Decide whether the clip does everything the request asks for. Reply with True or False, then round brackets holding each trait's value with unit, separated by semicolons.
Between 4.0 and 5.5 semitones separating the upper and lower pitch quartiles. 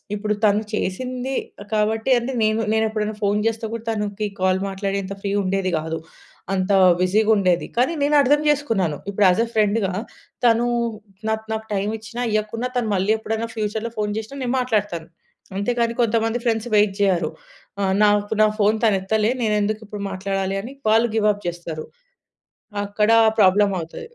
False (2.4 semitones)